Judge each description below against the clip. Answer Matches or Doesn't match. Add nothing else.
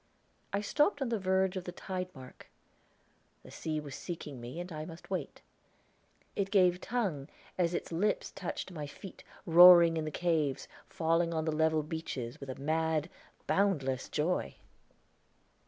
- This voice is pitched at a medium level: Matches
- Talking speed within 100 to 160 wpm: Matches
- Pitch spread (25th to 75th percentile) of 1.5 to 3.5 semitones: Matches